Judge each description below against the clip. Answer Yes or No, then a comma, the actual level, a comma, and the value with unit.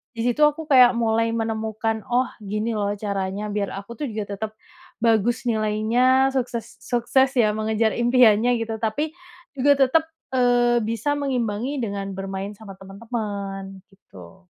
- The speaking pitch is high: Yes, high, 225 Hz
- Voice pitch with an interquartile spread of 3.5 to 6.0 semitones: No, average, 3.0 semitones